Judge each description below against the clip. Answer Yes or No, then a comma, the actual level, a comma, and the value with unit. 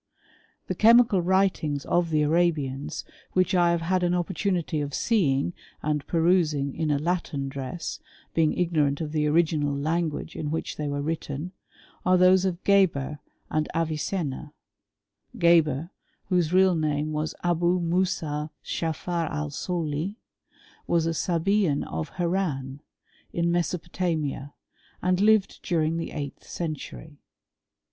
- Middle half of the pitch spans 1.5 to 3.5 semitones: Yes, average, 3.0 semitones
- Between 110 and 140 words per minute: Yes, slow, 135 wpm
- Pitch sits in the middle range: Yes, medium, 165 Hz